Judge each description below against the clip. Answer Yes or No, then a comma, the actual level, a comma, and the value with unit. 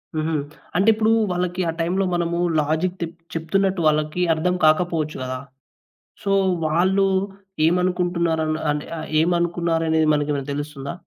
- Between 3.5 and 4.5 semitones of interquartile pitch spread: No, narrow, 2.5 semitones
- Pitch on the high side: No, medium, 170 Hz